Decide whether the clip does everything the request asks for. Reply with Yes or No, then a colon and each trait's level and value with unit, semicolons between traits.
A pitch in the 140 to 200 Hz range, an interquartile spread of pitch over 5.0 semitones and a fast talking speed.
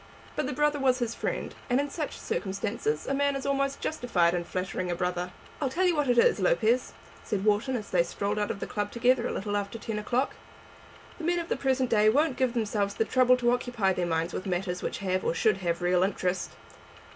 No: high, 215 Hz; wide, 5.6 semitones; fast, 225 wpm